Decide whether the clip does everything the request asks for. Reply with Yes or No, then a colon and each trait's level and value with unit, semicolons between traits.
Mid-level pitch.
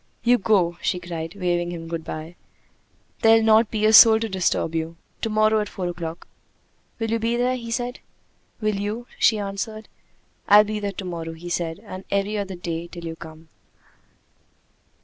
No: high, 195 Hz